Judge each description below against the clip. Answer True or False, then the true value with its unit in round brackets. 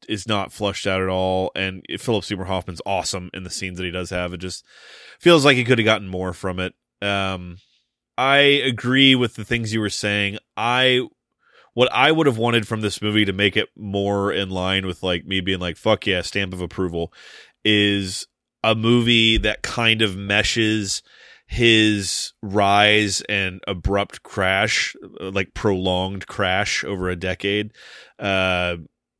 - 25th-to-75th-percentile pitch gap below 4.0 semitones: True (2.9 semitones)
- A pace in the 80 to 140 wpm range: False (170 wpm)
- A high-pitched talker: False (100 Hz)